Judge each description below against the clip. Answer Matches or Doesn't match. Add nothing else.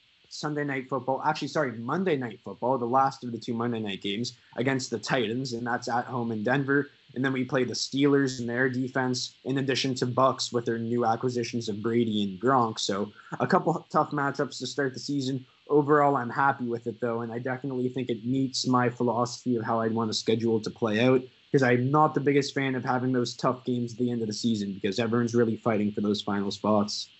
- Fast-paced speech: Matches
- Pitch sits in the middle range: Doesn't match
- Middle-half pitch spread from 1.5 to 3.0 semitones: Matches